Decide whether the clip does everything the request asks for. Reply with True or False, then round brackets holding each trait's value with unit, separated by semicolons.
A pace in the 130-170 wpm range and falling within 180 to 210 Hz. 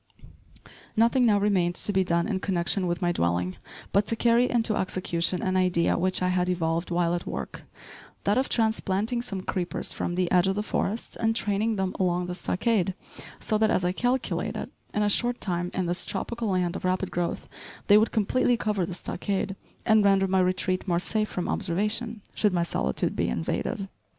False (190 wpm; 190 Hz)